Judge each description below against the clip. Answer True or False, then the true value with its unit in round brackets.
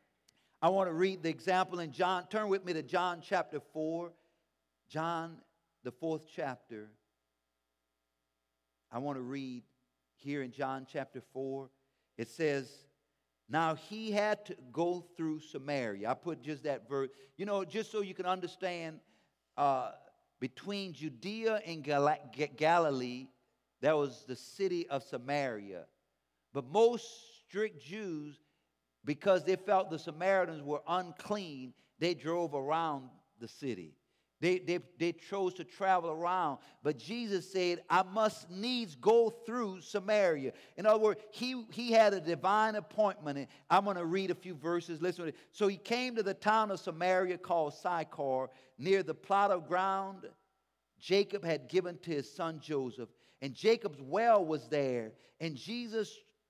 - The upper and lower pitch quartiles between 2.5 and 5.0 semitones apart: False (5.5 semitones)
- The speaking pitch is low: False (165 Hz)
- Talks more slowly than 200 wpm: True (150 wpm)